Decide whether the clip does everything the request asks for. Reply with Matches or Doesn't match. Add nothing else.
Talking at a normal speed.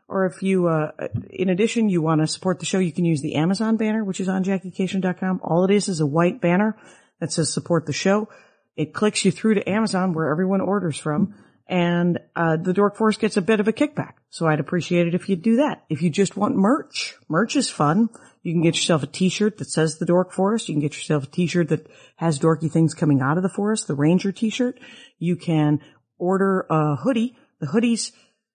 Doesn't match